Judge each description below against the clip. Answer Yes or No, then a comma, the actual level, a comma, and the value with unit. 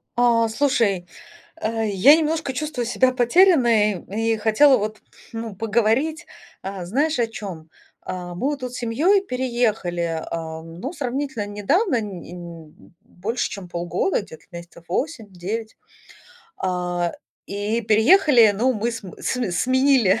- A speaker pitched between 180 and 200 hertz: No, high, 225 Hz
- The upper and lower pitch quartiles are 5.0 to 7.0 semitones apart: Yes, wide, 5.6 semitones